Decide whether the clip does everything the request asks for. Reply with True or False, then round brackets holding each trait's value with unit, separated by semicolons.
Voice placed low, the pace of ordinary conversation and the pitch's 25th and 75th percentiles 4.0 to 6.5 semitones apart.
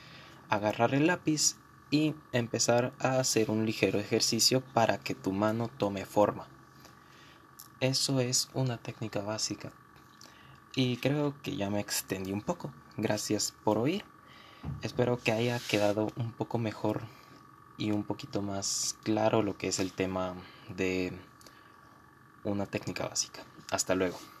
False (110 Hz; 135 wpm; 3.6 semitones)